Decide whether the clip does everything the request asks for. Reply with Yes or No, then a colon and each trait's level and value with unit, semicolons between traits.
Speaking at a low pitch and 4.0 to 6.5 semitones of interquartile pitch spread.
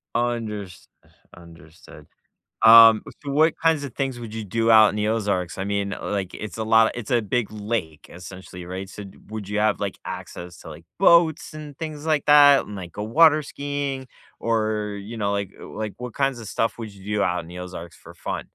Yes: low, 110 Hz; average, 4.4 semitones